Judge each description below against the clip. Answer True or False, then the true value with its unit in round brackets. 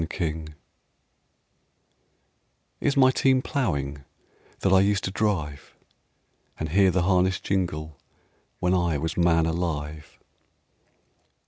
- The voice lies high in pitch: False (85 Hz)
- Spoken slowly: True (110 wpm)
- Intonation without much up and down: False (3.7 semitones)